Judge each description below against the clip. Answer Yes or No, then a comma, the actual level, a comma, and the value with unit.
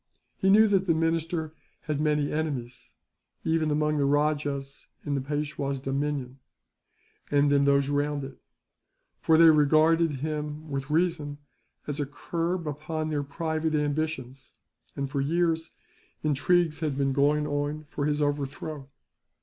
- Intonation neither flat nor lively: No, narrow, 2.0 semitones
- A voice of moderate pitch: Yes, medium, 150 Hz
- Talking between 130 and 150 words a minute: Yes, average, 140 wpm